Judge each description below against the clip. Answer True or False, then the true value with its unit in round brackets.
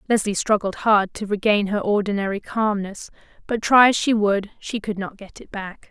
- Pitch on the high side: True (205 Hz)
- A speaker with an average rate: True (195 wpm)